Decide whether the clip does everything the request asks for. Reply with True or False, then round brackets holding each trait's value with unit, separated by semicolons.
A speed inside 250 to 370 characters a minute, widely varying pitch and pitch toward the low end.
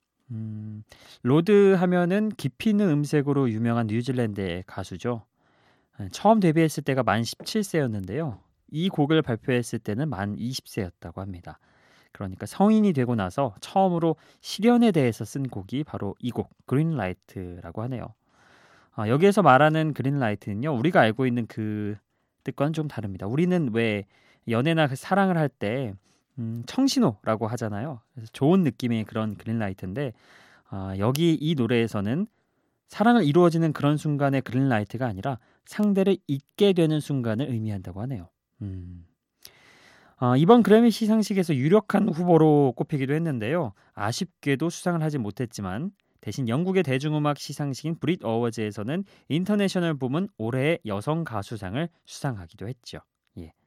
True (330 characters per minute; 6.9 semitones; 130 Hz)